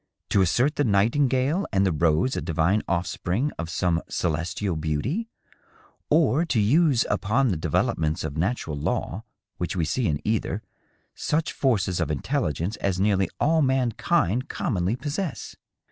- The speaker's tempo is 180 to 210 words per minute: No, average, 150 wpm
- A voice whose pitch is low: Yes, low, 100 Hz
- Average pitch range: No, wide, 7.7 semitones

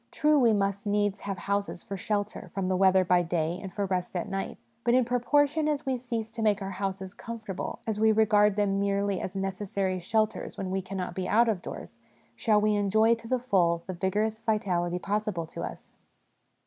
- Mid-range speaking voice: No, high, 200 Hz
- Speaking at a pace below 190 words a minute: No, fast, 205 wpm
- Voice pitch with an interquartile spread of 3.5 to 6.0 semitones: No, average, 2.7 semitones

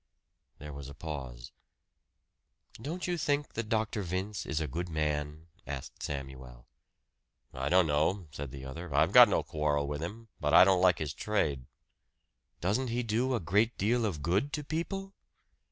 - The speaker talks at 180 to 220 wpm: No, average, 170 wpm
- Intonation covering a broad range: Yes, wide, 7.2 semitones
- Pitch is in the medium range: No, very low, 85 Hz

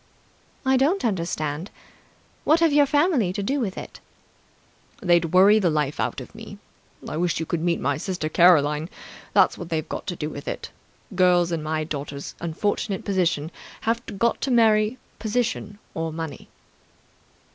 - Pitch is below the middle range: No, medium, 180 Hz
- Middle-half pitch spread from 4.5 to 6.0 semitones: Yes, wide, 5.6 semitones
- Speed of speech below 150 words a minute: No, average, 165 wpm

